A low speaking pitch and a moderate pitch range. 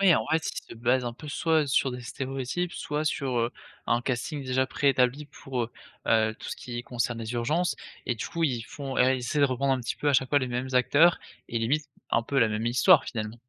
Yes: low, 130 Hz; average, 3.3 semitones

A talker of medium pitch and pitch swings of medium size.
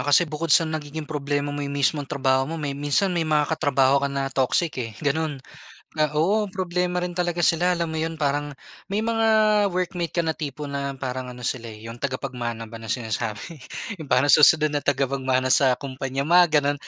Yes: medium, 145 Hz; average, 3.5 semitones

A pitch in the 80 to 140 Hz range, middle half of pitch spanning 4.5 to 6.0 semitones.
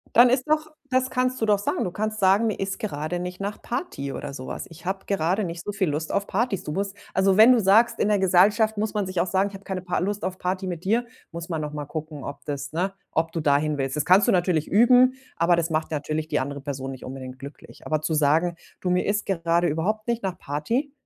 No: medium, 185 Hz; average, 4.9 semitones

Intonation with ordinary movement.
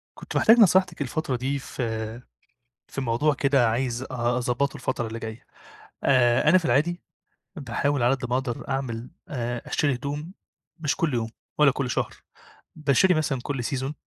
Yes: average, 3.4 semitones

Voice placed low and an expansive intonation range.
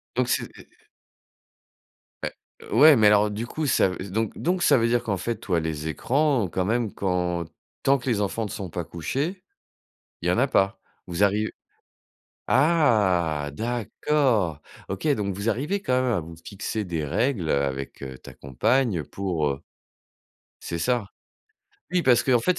Yes: low, 105 Hz; wide, 6.4 semitones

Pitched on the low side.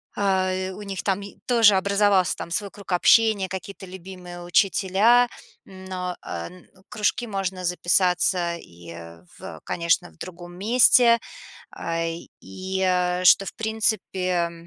No: high, 190 Hz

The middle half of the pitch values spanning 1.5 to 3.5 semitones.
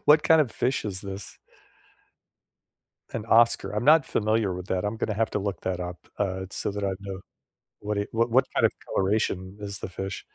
Yes: average, 2.9 semitones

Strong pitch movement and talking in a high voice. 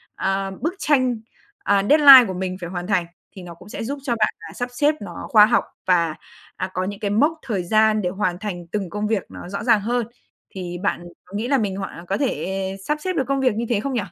No: average, 4.8 semitones; high, 210 Hz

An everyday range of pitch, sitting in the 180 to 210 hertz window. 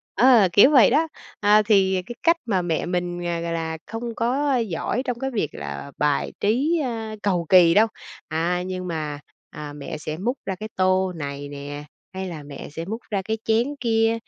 No: wide, 5.7 semitones; high, 190 Hz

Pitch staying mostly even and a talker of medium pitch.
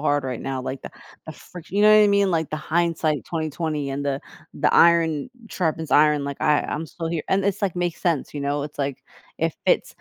No: average, 3.1 semitones; medium, 155 Hz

